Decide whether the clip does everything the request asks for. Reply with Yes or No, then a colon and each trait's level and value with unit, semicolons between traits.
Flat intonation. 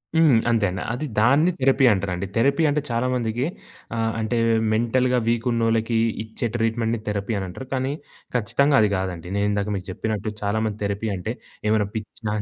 No: average, 3.2 semitones